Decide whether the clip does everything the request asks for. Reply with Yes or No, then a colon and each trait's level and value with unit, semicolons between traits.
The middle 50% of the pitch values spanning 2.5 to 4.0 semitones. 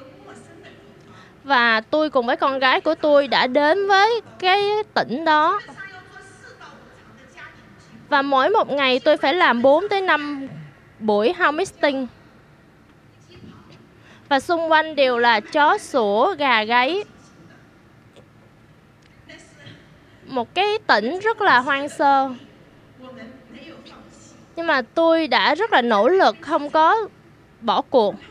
No: average, 4.9 semitones